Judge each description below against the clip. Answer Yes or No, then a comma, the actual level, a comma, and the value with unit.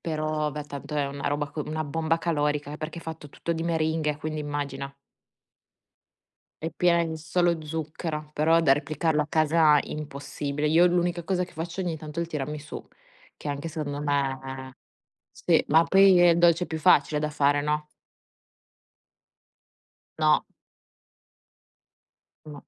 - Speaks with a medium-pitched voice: Yes, medium, 155 Hz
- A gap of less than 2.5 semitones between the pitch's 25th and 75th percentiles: Yes, narrow, 2.0 semitones